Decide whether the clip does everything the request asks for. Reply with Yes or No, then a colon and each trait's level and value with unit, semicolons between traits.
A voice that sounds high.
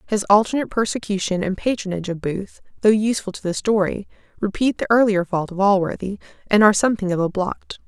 Yes: high, 200 Hz